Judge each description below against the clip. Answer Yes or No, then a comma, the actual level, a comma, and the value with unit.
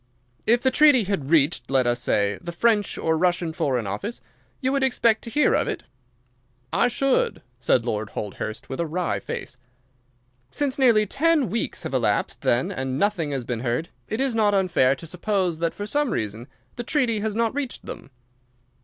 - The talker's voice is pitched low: No, medium, 185 Hz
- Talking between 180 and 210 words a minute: Yes, average, 185 wpm